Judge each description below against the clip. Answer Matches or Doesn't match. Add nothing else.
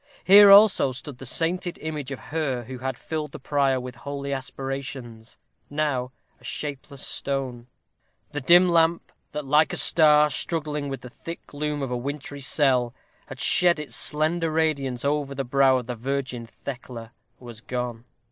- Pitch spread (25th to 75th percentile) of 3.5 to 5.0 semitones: Doesn't match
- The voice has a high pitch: Doesn't match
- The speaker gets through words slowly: Doesn't match